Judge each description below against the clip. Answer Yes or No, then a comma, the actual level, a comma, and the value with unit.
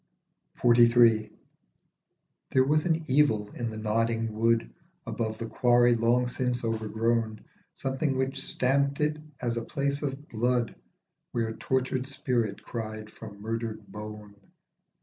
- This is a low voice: Yes, low, 120 Hz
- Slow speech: Yes, slow, 130 wpm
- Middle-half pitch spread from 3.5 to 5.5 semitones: No, average, 3.0 semitones